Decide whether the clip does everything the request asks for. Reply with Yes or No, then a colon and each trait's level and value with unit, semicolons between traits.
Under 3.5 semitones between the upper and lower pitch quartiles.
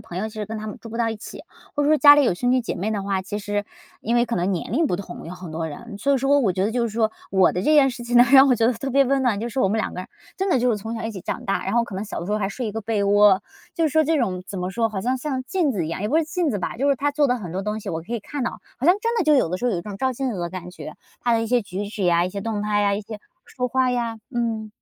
No: average, 4.3 semitones